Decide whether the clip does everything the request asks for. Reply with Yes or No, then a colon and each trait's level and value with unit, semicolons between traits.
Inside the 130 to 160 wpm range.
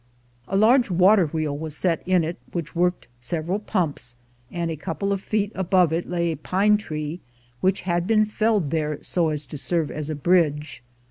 No: average, 190 wpm